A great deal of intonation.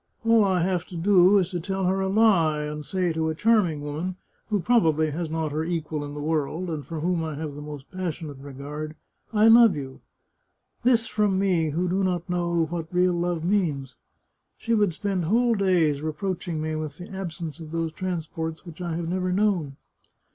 No: average, 3.3 semitones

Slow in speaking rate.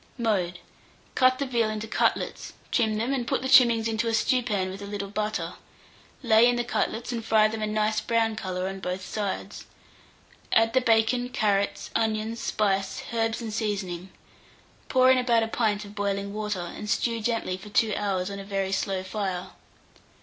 No: average, 180 wpm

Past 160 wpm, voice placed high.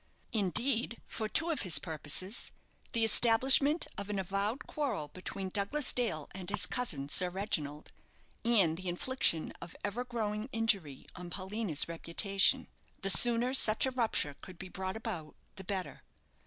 No: average, 150 wpm; high, 200 Hz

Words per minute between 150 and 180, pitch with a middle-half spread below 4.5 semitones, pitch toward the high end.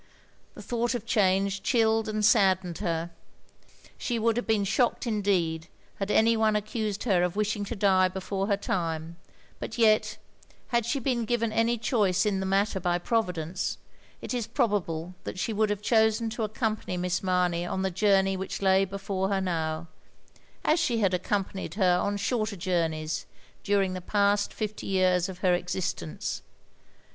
Yes: average, 170 wpm; average, 3.2 semitones; high, 195 Hz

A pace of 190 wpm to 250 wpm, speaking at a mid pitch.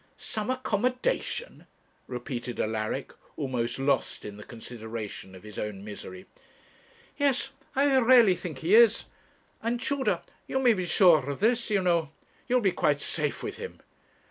No: average, 150 wpm; medium, 170 Hz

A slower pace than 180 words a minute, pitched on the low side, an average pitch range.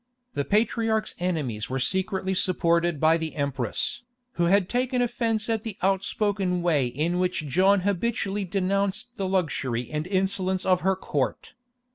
No: average, 145 wpm; medium, 185 Hz; average, 3.8 semitones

